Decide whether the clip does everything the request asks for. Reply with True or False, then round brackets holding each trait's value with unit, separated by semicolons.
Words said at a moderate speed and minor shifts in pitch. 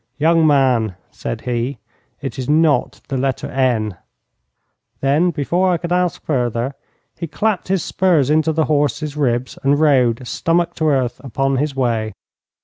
False (150 wpm; 4.2 semitones)